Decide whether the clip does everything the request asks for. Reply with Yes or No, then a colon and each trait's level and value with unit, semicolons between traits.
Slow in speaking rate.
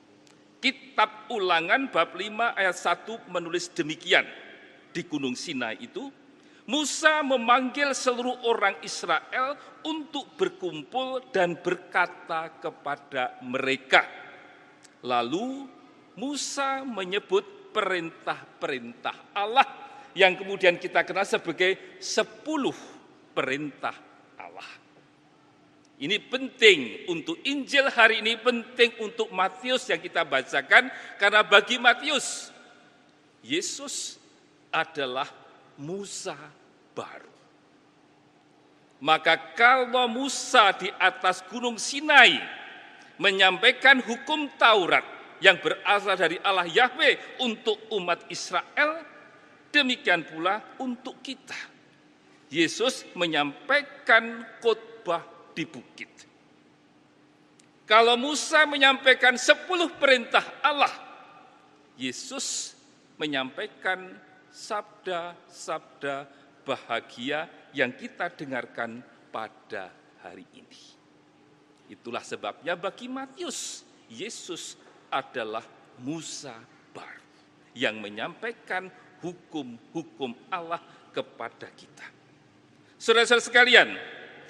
Yes: slow, 80 wpm